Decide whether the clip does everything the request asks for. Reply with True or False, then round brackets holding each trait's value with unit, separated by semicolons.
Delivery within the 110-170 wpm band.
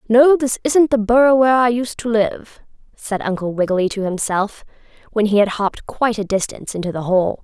False (200 wpm)